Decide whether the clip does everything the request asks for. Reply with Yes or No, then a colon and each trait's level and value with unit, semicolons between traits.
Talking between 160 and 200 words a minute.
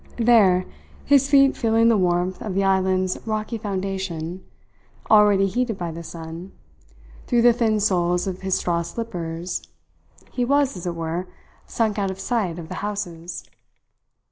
No: average, 150 wpm